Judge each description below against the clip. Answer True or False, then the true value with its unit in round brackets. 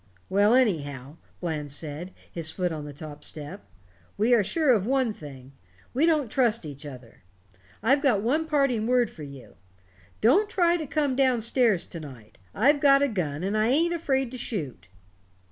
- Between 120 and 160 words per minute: False (180 wpm)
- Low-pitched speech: False (215 Hz)